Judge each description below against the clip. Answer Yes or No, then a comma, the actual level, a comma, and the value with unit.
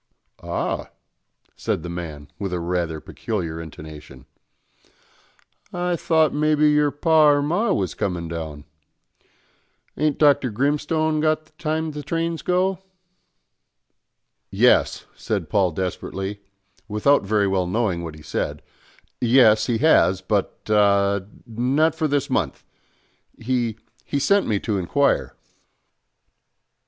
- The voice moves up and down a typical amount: No, wide, 8.7 semitones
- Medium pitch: No, low, 115 Hz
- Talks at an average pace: No, slow, 120 wpm